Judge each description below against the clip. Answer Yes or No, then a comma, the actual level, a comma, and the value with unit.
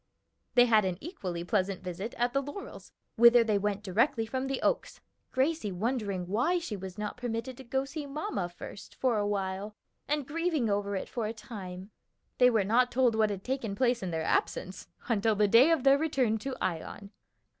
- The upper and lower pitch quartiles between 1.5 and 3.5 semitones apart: No, average, 4.7 semitones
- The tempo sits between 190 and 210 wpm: Yes, average, 200 wpm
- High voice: Yes, high, 225 Hz